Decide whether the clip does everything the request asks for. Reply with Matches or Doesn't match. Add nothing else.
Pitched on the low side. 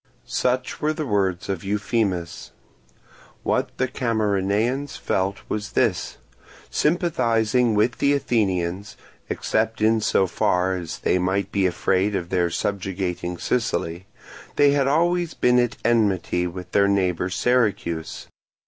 Matches